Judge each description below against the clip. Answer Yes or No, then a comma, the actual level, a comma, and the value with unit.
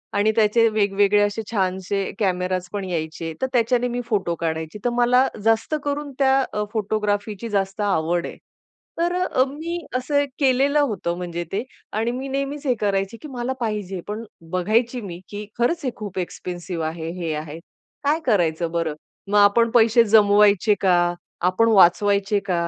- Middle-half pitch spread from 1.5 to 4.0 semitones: No, average, 4.7 semitones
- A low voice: No, high, 210 Hz